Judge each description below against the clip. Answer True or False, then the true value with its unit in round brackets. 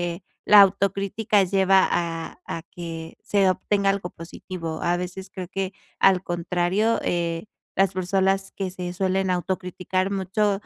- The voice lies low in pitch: False (185 Hz)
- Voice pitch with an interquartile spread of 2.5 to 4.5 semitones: False (1.8 semitones)